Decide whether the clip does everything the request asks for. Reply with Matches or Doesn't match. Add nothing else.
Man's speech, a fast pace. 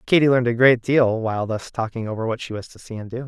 Matches